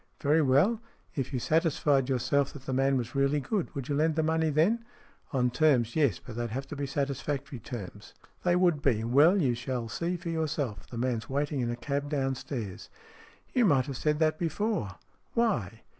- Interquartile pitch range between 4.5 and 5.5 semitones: No, average, 4.0 semitones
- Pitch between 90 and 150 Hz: Yes, medium, 140 Hz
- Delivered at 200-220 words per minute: Yes, fast, 205 wpm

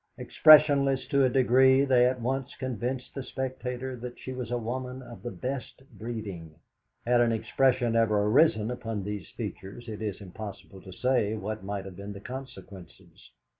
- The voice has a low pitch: Yes, low, 120 Hz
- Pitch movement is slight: No, average, 3.8 semitones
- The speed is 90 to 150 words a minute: No, average, 170 wpm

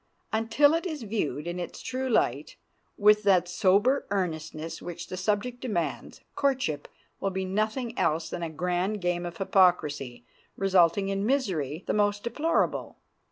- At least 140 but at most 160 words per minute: Yes, average, 150 wpm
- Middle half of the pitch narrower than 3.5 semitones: No, average, 4.5 semitones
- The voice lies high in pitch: Yes, high, 195 Hz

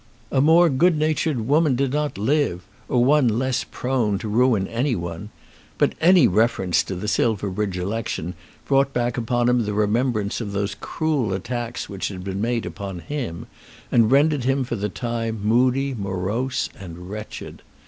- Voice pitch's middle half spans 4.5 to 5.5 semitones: Yes, average, 4.9 semitones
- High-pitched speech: No, low, 115 Hz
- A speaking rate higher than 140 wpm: Yes, average, 165 wpm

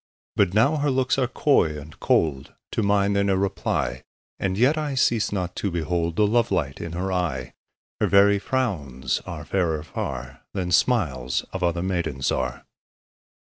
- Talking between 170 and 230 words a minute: Yes, average, 175 wpm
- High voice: No, very low, 90 Hz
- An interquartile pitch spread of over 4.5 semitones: Yes, average, 5.3 semitones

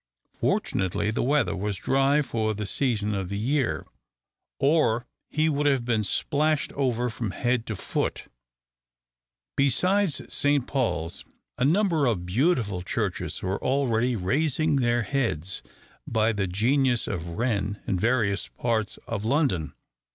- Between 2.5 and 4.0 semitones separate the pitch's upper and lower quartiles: No, wide, 5.4 semitones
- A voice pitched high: No, low, 120 Hz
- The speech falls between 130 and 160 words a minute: Yes, slow, 135 wpm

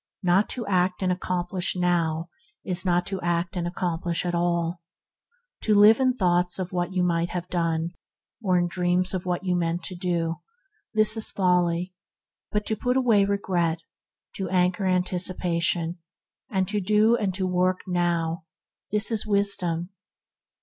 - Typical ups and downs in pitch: No, narrow, 1.9 semitones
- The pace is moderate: Yes, average, 155 wpm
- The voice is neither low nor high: Yes, medium, 180 Hz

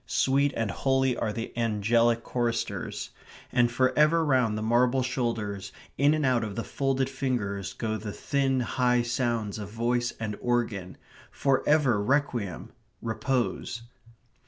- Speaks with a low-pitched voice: Yes, low, 120 Hz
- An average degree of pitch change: Yes, average, 3.1 semitones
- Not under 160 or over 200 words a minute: No, average, 140 wpm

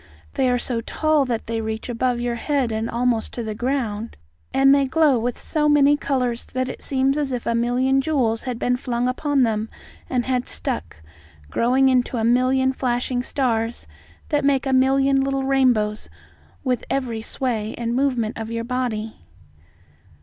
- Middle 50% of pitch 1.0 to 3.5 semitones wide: Yes, narrow, 2.6 semitones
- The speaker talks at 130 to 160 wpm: No, average, 170 wpm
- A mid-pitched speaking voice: No, very high, 250 Hz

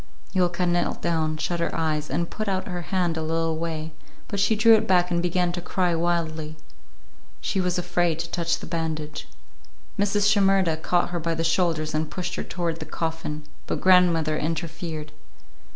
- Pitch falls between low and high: Yes, medium, 170 Hz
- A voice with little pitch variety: Yes, narrow, 2.0 semitones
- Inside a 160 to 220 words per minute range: Yes, average, 180 wpm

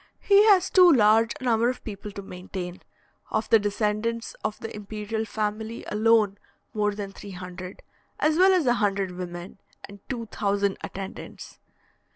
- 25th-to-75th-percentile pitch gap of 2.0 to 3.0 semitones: Yes, narrow, 2.6 semitones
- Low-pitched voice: No, high, 210 Hz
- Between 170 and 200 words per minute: No, average, 160 wpm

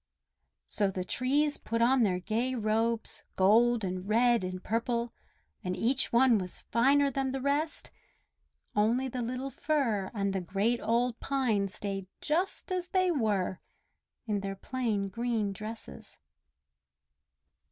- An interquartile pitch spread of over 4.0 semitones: Yes, average, 4.5 semitones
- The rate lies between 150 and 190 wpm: No, slow, 135 wpm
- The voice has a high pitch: Yes, high, 230 Hz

